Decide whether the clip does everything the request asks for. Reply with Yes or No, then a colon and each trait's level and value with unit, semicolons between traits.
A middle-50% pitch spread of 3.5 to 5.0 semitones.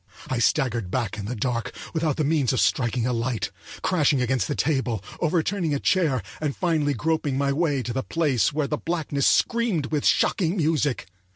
Yes: average, 4.3 semitones